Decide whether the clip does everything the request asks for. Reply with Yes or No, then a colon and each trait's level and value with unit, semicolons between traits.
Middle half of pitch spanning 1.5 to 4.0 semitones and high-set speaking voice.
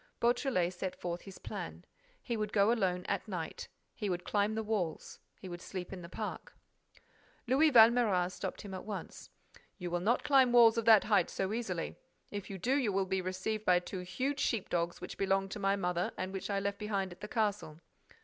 Yes: average, 3.3 semitones; high, 195 Hz